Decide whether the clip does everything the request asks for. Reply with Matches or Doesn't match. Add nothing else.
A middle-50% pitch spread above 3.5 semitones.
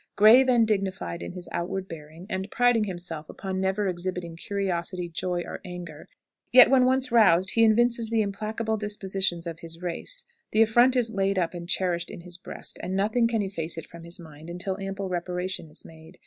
Matches